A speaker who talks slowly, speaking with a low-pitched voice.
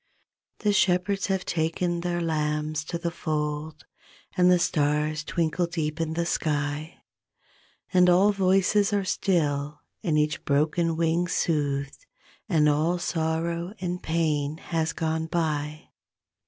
No: slow, 125 wpm; medium, 165 Hz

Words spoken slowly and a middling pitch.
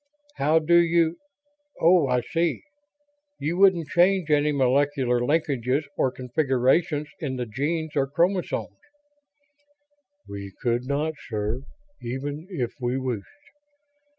Yes: slow, 115 wpm; medium, 145 Hz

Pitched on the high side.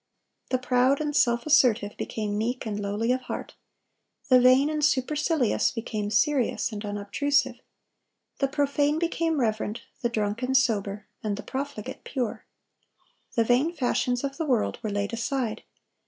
Yes: very high, 250 Hz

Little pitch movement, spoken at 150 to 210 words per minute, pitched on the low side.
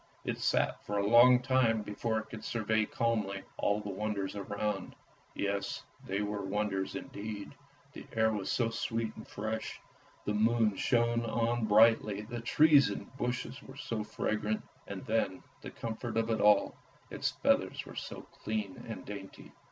Yes: narrow, 2.1 semitones; average, 160 wpm; low, 110 Hz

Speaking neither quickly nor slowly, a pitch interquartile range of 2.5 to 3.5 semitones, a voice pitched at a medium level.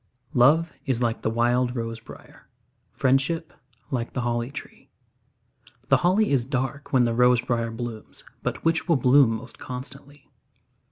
No: average, 150 wpm; average, 3.0 semitones; low, 125 Hz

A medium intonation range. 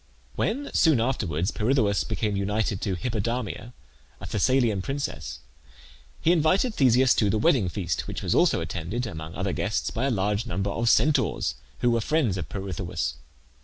Yes: average, 5.0 semitones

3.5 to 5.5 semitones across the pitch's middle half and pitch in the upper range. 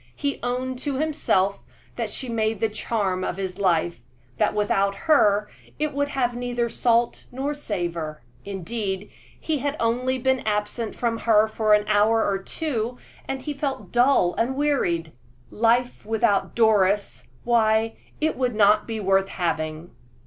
Yes: average, 4.1 semitones; high, 225 Hz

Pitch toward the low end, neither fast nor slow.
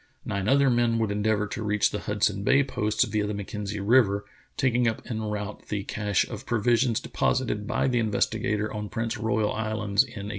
Yes: low, 110 Hz; average, 190 wpm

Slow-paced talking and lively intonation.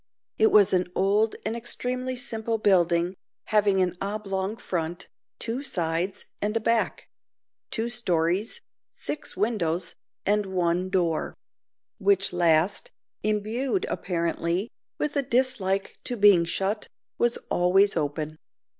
No: slow, 120 wpm; average, 4.2 semitones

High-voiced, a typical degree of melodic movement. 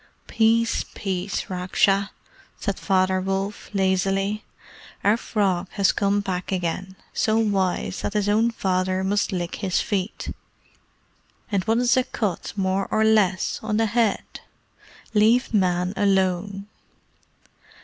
No: high, 195 Hz; narrow, 2.2 semitones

